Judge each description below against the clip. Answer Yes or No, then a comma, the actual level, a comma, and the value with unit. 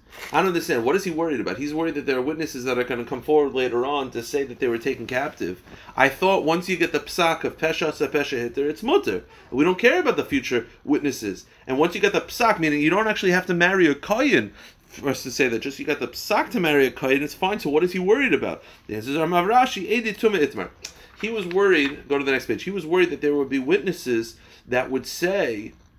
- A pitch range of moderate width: No, wide, 5.9 semitones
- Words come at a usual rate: No, fast, 255 wpm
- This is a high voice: No, medium, 155 Hz